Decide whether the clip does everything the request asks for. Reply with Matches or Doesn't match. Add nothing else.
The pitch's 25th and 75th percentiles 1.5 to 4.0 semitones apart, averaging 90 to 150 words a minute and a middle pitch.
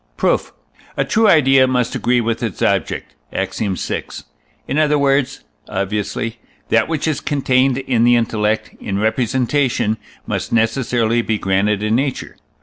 Doesn't match